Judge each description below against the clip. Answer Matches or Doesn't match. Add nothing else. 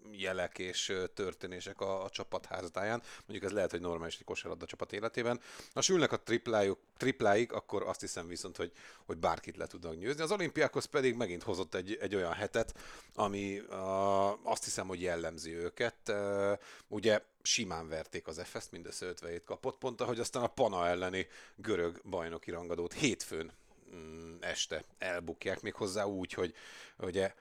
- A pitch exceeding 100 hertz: Doesn't match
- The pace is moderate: Doesn't match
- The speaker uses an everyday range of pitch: Matches